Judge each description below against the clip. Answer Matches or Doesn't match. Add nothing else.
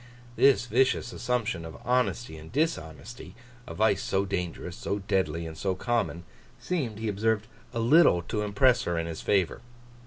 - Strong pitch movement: Matches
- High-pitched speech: Doesn't match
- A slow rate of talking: Doesn't match